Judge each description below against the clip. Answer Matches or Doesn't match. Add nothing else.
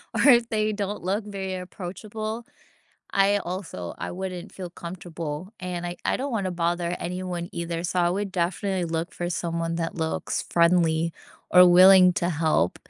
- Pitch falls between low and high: Matches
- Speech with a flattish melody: Matches